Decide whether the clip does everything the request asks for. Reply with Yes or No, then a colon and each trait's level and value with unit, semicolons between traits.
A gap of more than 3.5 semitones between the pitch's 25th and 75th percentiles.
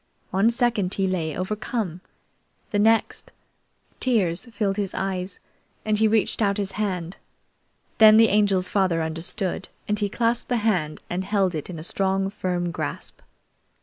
No: average, 2.9 semitones